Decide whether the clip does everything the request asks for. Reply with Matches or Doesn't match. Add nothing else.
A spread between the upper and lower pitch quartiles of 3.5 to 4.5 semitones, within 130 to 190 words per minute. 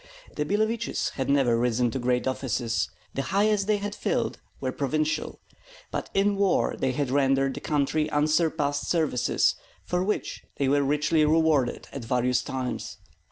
Matches